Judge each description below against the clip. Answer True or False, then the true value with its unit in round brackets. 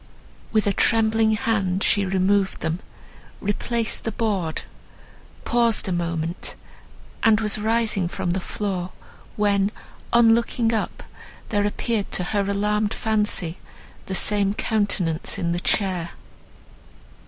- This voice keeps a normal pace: False (120 wpm)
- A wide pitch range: False (2.9 semitones)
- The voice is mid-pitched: False (205 Hz)